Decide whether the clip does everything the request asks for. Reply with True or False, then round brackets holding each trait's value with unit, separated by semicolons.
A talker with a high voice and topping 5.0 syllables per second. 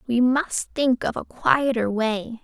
False (240 Hz; 3.8 syllables/s)